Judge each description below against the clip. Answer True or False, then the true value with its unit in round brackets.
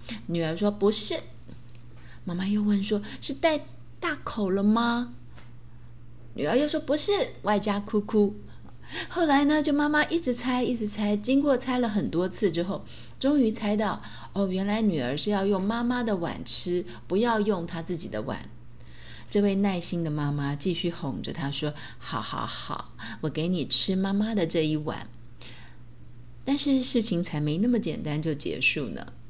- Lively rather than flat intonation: True (7.4 semitones)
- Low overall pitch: False (195 Hz)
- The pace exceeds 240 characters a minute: False (230 characters per minute)